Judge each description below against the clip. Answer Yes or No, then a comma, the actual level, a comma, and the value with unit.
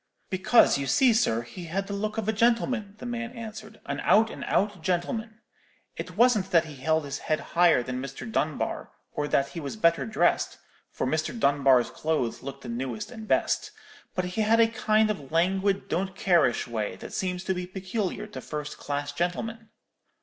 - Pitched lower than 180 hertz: No, medium, 185 Hz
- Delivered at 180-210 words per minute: Yes, average, 185 wpm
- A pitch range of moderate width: No, wide, 6.9 semitones